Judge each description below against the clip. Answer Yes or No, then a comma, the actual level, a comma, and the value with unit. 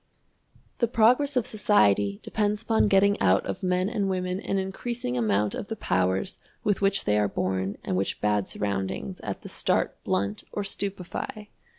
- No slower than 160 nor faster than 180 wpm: Yes, average, 170 wpm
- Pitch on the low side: No, medium, 185 Hz